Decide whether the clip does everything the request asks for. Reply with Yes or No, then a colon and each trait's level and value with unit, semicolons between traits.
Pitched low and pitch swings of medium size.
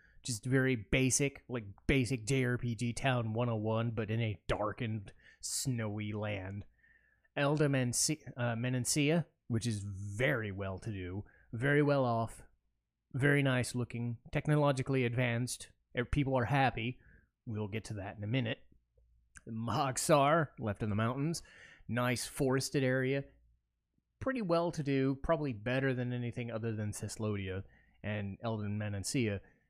Yes: low, 120 Hz; average, 3.9 semitones